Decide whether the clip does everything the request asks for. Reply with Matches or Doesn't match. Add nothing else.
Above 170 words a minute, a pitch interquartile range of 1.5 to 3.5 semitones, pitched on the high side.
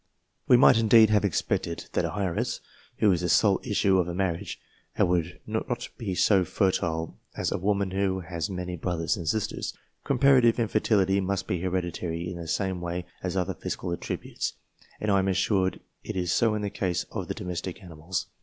Doesn't match